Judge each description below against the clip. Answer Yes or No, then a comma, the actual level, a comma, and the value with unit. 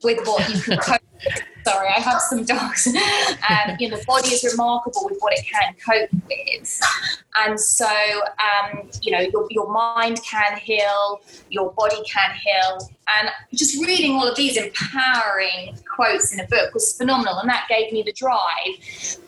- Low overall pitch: No, high, 220 Hz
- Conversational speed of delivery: Yes, average, 175 wpm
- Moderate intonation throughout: Yes, average, 3.8 semitones